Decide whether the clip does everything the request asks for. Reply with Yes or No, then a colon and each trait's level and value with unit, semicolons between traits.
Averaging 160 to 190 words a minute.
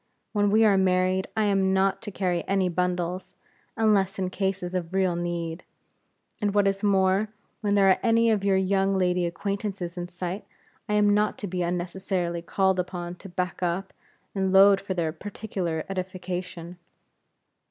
Yes: average, 165 wpm